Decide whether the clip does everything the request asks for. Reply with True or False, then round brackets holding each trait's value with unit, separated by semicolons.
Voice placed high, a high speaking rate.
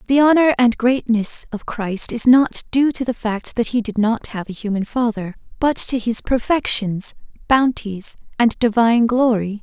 False (235 Hz; 175 wpm)